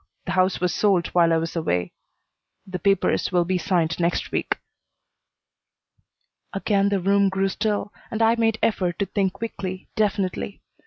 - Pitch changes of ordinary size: No, narrow, 2.3 semitones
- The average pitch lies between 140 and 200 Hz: Yes, high, 190 Hz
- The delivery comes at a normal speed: Yes, average, 155 wpm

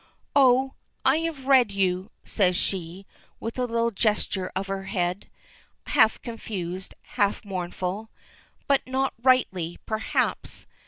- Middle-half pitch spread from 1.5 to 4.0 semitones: No, average, 5.2 semitones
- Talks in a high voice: Yes, high, 210 Hz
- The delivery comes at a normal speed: No, slow, 120 wpm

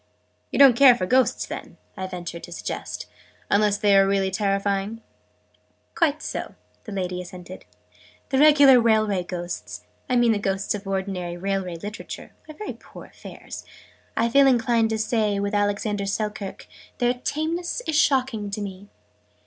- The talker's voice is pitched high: Yes, high, 205 Hz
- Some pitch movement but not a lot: Yes, average, 4.0 semitones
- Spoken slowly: No, average, 155 wpm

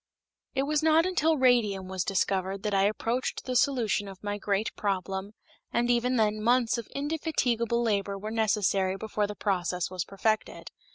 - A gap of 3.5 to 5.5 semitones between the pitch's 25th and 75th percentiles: Yes, average, 3.8 semitones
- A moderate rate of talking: Yes, average, 165 wpm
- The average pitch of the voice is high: Yes, high, 215 Hz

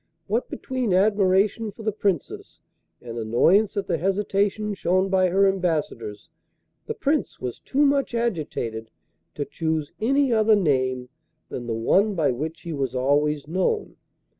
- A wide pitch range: Yes, wide, 6.8 semitones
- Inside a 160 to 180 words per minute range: No, average, 145 wpm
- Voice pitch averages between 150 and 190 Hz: Yes, medium, 185 Hz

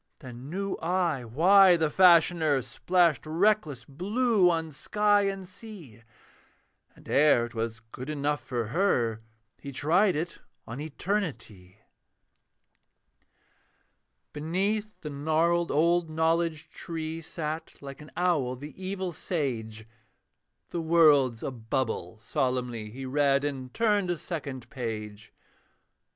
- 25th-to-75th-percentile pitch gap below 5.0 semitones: No, wide, 5.6 semitones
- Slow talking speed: Yes, slow, 115 wpm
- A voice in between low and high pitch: Yes, medium, 155 Hz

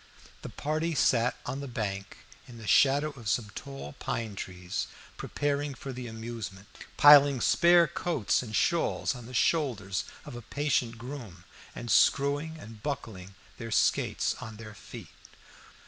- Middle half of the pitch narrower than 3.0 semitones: No, average, 4.9 semitones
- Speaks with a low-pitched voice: Yes, low, 120 Hz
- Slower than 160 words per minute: Yes, average, 145 wpm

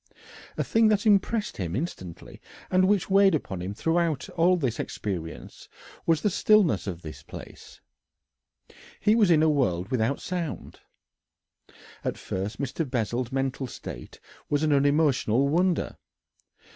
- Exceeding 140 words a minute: No, slow, 135 wpm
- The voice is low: No, medium, 145 Hz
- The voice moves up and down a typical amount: No, wide, 8.0 semitones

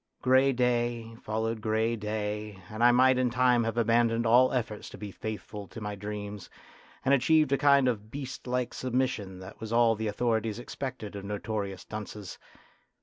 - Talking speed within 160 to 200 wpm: Yes, average, 170 wpm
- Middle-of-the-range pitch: No, low, 115 Hz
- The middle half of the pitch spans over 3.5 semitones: No, average, 2.9 semitones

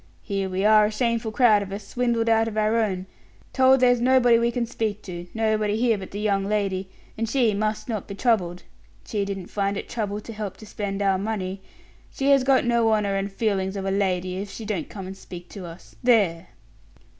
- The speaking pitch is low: No, high, 210 Hz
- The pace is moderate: No, fast, 215 wpm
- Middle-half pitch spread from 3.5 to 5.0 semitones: No, average, 2.7 semitones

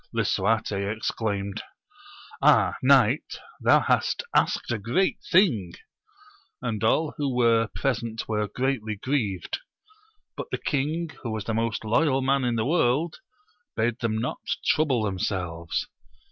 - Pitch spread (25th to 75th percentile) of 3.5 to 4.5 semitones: Yes, average, 4.0 semitones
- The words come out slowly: Yes, slow, 130 wpm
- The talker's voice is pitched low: Yes, low, 115 Hz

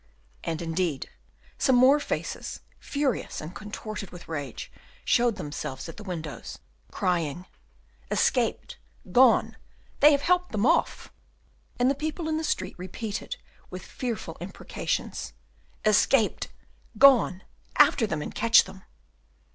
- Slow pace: Yes, slow, 125 wpm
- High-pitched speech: Yes, high, 210 Hz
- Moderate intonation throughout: No, wide, 7.2 semitones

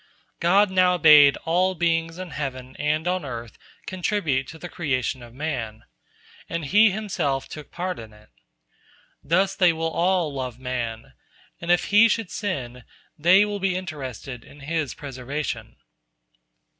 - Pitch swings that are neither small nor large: No, wide, 5.7 semitones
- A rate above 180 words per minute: No, average, 150 wpm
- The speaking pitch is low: No, medium, 160 Hz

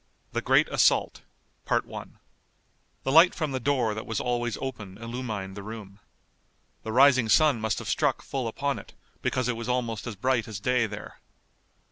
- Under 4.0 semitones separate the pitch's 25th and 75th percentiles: Yes, average, 3.0 semitones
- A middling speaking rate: Yes, average, 165 wpm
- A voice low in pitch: Yes, low, 120 Hz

